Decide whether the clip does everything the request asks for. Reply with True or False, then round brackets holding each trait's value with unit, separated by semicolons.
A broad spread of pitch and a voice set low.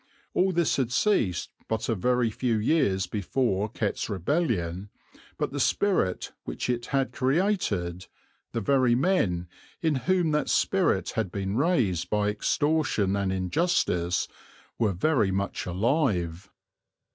True (7.5 semitones; 110 Hz)